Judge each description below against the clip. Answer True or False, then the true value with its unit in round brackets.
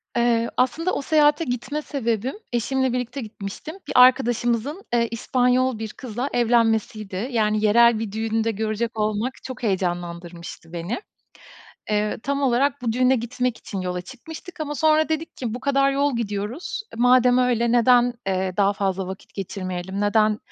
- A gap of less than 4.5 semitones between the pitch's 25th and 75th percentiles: True (3.5 semitones)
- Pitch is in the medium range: False (235 Hz)